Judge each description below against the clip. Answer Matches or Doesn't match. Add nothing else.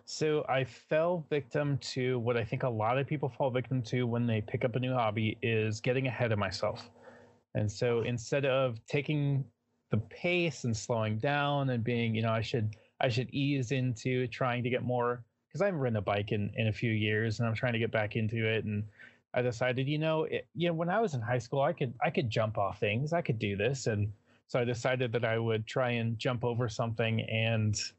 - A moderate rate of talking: Doesn't match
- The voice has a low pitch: Matches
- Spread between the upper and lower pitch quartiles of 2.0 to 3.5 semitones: Matches